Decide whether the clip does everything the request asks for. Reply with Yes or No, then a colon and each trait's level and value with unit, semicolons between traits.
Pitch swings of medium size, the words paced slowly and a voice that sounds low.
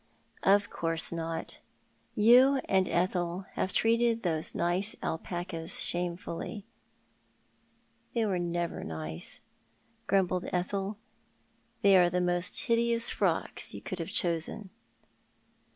No: average, 3.1 semitones; slow, 115 wpm; medium, 180 Hz